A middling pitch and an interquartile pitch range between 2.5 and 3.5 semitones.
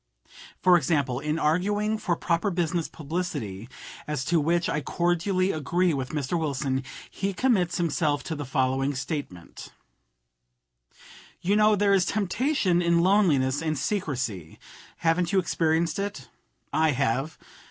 No: medium, 165 Hz; average, 4.4 semitones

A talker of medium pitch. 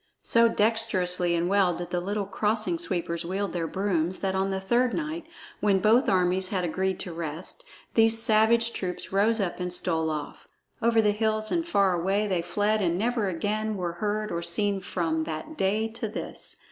No: high, 195 Hz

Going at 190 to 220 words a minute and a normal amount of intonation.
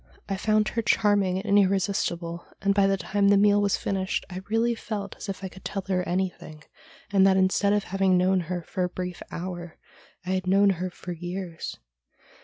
No: average, 200 wpm; narrow, 1.7 semitones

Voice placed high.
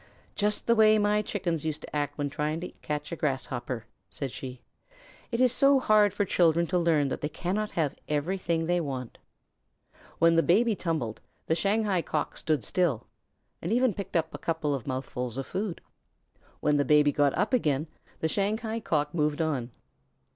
No: medium, 165 Hz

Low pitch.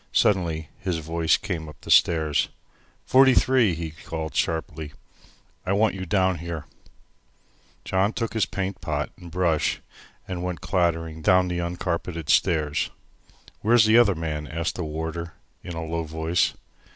Yes: very low, 85 Hz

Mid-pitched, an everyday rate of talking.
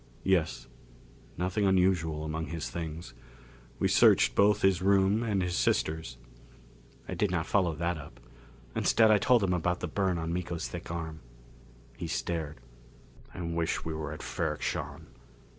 No: very low, 85 Hz; average, 155 wpm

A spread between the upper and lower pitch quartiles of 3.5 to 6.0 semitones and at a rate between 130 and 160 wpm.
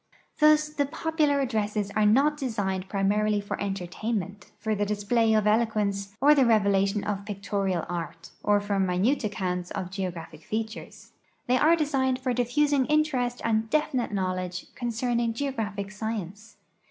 Yes: average, 4.1 semitones; average, 140 wpm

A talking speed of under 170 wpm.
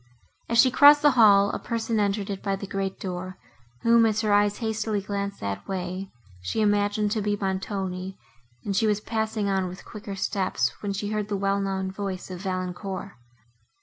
No: average, 185 wpm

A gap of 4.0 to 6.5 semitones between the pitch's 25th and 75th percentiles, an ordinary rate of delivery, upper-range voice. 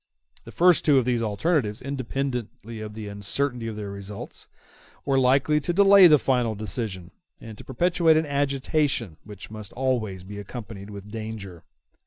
No: average, 5.1 semitones; average, 160 wpm; low, 115 Hz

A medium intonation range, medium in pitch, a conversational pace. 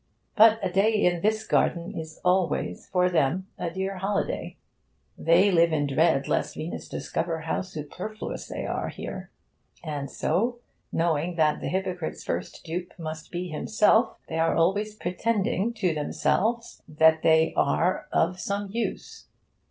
Yes: average, 3.9 semitones; medium, 180 Hz; average, 145 wpm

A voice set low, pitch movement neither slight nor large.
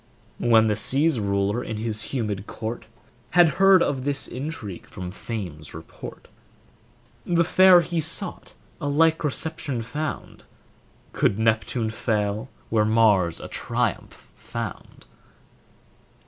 No: low, 115 Hz; wide, 6.6 semitones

